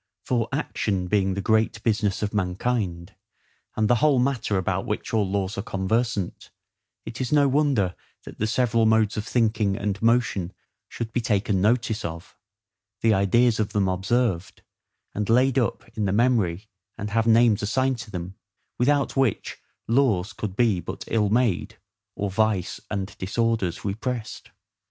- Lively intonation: No, average, 3.3 semitones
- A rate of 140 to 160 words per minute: Yes, average, 155 wpm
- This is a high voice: No, low, 110 Hz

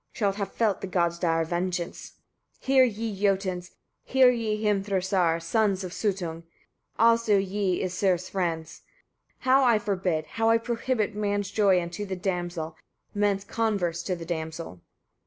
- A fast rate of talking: No, average, 145 wpm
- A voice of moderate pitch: No, high, 195 Hz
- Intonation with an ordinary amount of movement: Yes, average, 3.4 semitones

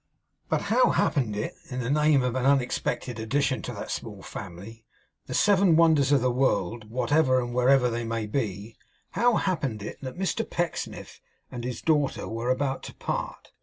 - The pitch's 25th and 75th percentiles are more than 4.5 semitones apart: No, average, 3.9 semitones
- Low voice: Yes, low, 125 Hz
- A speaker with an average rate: Yes, average, 175 wpm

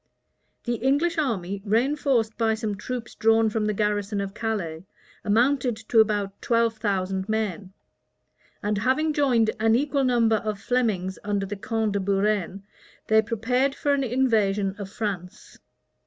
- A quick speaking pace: No, average, 145 wpm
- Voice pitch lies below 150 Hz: No, high, 220 Hz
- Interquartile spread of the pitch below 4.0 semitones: Yes, average, 3.2 semitones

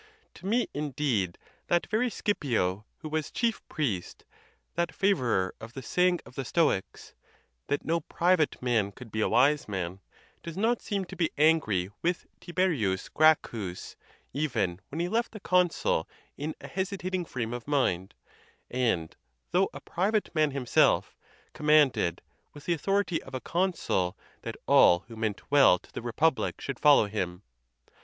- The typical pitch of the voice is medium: Yes, medium, 145 Hz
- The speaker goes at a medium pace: Yes, average, 160 wpm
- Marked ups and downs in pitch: Yes, wide, 8.1 semitones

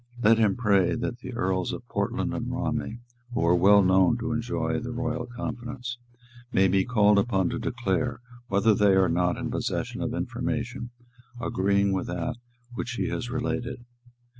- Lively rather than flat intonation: No, average, 4.1 semitones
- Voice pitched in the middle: No, low, 115 Hz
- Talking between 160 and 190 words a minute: Yes, average, 165 wpm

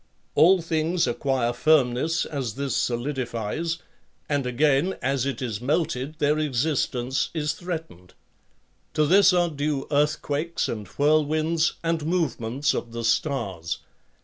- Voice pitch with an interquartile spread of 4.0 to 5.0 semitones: Yes, average, 4.3 semitones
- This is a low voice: No, medium, 145 Hz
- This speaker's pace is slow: Yes, slow, 120 wpm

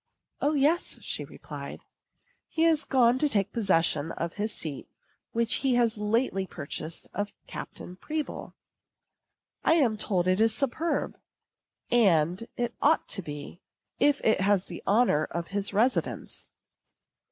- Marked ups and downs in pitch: Yes, wide, 6.1 semitones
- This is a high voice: Yes, high, 215 Hz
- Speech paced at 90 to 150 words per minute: Yes, average, 140 wpm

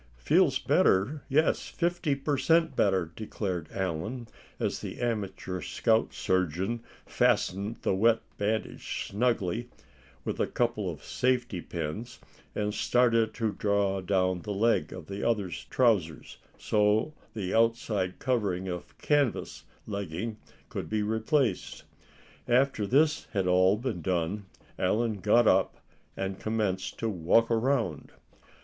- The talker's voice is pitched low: Yes, low, 105 Hz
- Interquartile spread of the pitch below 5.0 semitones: Yes, average, 4.0 semitones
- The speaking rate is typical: No, slow, 125 wpm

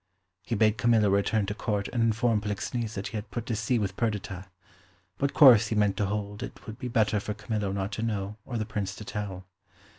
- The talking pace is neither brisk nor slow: No, fast, 220 wpm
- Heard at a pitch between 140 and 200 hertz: No, low, 105 Hz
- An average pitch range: No, narrow, 2.0 semitones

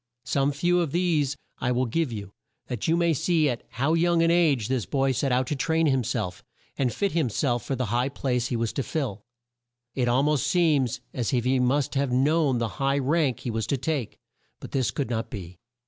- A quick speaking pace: Yes, fast, 225 wpm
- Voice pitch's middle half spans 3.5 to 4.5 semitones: Yes, average, 4.0 semitones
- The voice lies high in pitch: No, low, 135 Hz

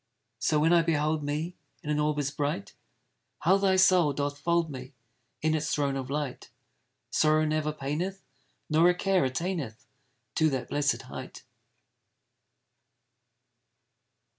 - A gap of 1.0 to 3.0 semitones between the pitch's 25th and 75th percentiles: Yes, average, 2.7 semitones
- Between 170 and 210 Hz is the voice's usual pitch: No, medium, 150 Hz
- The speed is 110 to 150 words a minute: Yes, slow, 135 wpm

